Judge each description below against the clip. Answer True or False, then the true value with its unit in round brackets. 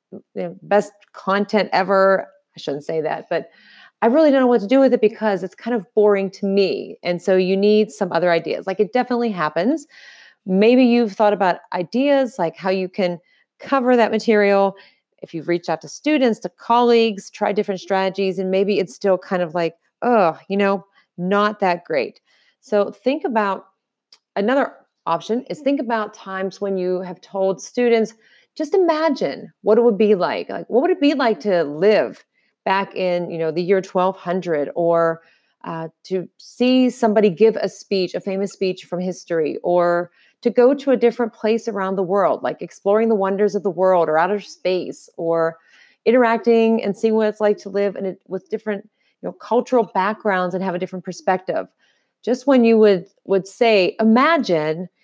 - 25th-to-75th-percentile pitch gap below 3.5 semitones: False (3.8 semitones)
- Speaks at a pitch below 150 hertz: False (200 Hz)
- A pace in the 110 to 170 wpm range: False (185 wpm)